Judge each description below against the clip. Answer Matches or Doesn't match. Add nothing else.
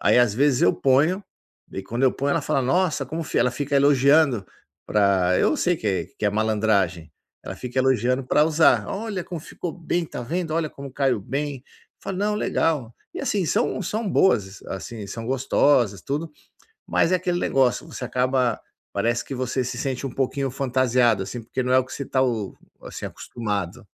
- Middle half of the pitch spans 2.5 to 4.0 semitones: Doesn't match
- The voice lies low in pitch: Matches